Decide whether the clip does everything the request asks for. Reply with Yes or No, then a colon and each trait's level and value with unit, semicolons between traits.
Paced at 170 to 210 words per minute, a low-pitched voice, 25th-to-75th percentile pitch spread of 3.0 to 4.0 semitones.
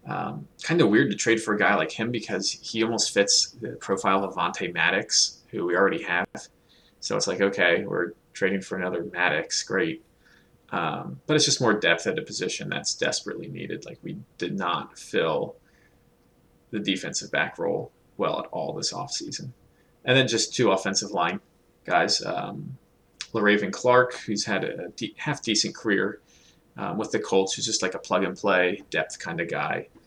Yes: average, 185 wpm; low, 110 Hz; average, 3.7 semitones